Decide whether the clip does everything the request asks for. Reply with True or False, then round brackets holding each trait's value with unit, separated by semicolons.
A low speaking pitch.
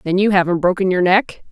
False (185 Hz)